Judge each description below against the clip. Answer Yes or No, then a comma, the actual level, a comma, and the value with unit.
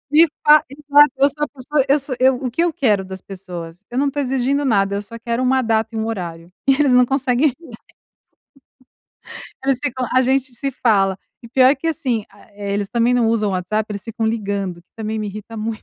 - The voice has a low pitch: No, high, 235 Hz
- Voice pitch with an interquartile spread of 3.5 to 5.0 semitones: Yes, average, 4.6 semitones